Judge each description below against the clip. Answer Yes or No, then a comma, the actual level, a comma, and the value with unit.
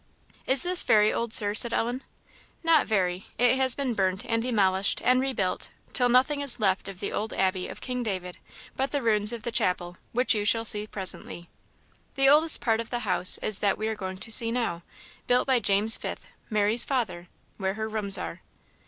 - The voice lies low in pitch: No, high, 220 Hz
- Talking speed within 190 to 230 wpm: Yes, average, 200 wpm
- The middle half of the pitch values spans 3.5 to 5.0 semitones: Yes, average, 4.1 semitones